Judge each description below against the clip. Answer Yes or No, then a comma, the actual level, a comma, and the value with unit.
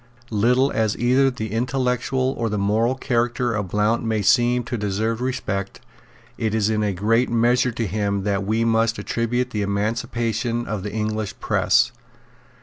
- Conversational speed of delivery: Yes, average, 160 wpm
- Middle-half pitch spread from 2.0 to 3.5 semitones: Yes, narrow, 2.6 semitones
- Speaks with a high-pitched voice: No, low, 115 Hz